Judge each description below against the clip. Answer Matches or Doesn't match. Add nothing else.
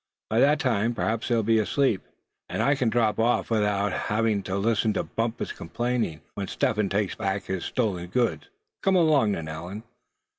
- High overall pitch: Doesn't match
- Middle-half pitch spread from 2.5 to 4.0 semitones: Matches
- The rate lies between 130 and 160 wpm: Doesn't match